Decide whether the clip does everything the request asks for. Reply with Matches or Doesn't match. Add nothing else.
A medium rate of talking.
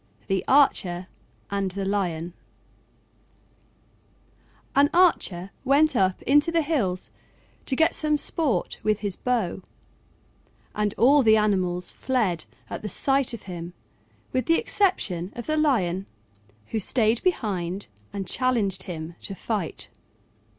Doesn't match